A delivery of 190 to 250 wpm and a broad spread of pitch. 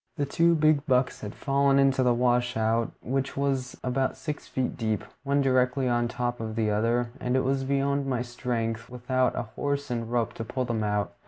No: average, 195 wpm; average, 2.7 semitones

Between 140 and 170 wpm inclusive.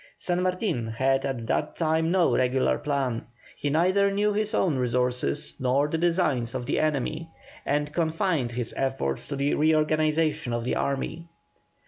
Yes: average, 155 wpm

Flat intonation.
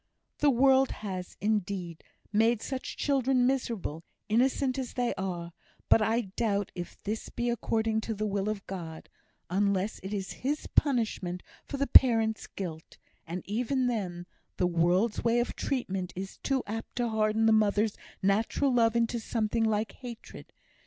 No: average, 3.7 semitones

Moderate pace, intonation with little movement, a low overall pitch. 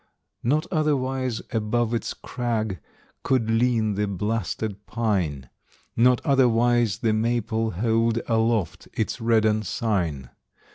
No: slow, 105 wpm; narrow, 2.1 semitones; low, 115 Hz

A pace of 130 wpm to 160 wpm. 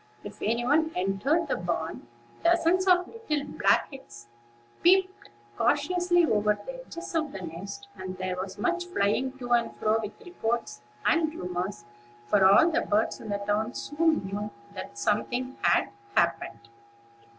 Yes: average, 150 wpm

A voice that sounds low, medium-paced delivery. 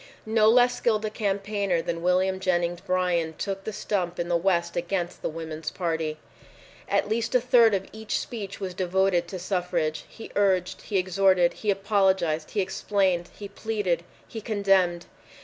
No: high, 190 Hz; average, 165 wpm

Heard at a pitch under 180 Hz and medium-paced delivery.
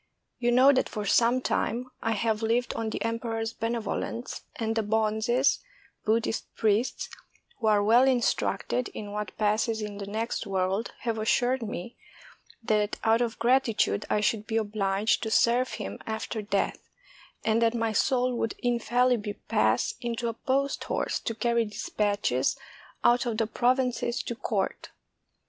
No: high, 225 Hz; average, 155 wpm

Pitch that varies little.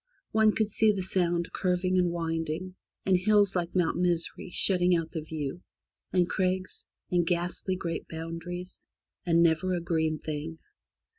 Yes: narrow, 2.0 semitones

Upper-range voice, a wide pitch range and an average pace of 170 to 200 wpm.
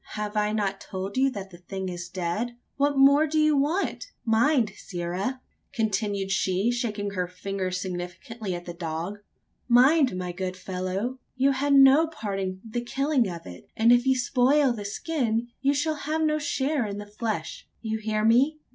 Yes: high, 220 Hz; wide, 6.0 semitones; average, 180 wpm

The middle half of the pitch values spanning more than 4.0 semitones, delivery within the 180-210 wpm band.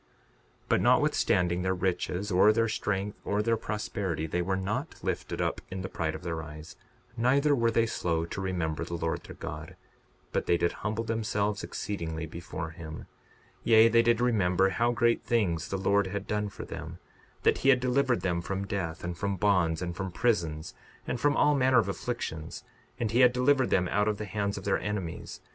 Yes: average, 4.8 semitones; average, 200 wpm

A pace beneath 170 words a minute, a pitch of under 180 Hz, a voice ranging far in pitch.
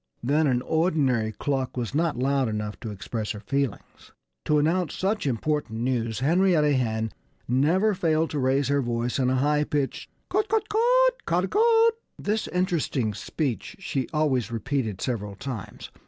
Yes: average, 160 wpm; medium, 140 Hz; wide, 5.9 semitones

